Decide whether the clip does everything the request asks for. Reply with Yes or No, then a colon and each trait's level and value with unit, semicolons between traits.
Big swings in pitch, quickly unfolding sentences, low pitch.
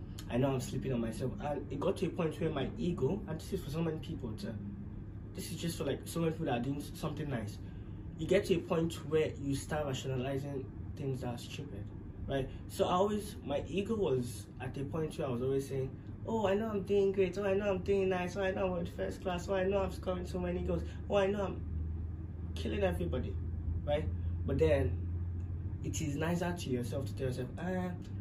Yes: wide, 8.8 semitones; fast, 230 wpm; low, 115 Hz